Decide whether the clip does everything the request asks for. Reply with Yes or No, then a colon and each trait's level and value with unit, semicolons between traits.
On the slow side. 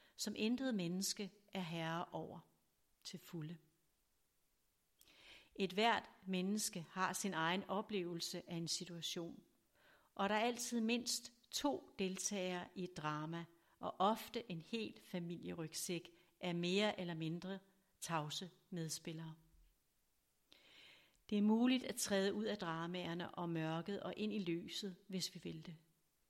Yes: slow, 130 wpm